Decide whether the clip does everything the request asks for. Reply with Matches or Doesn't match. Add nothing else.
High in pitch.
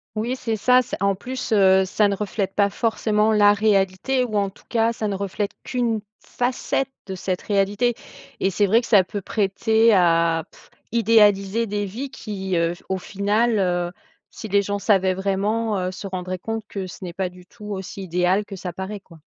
Matches